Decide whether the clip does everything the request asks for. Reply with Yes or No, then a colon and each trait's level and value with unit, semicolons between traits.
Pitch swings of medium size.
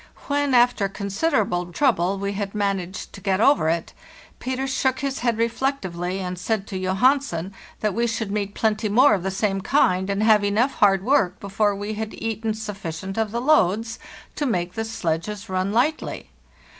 Yes: average, 3.7 semitones